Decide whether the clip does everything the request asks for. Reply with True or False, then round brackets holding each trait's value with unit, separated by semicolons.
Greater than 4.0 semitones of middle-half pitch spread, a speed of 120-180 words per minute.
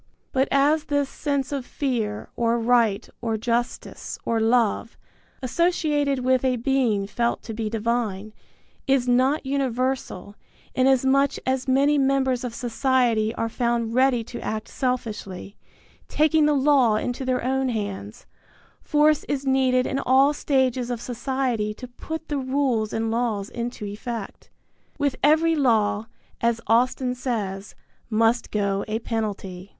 False (3.2 semitones; 135 wpm)